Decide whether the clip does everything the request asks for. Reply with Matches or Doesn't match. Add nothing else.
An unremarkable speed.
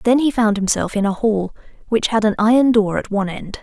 Doesn't match